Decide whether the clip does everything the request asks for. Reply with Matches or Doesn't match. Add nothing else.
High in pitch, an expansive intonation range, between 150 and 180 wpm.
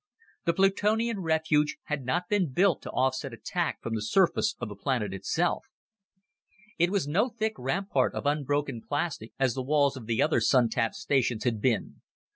Doesn't match